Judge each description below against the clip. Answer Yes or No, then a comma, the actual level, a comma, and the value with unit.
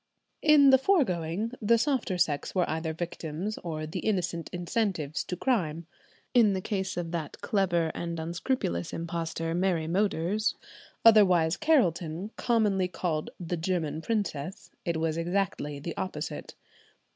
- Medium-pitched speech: Yes, medium, 175 Hz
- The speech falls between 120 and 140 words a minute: Yes, slow, 135 wpm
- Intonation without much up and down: No, average, 4.0 semitones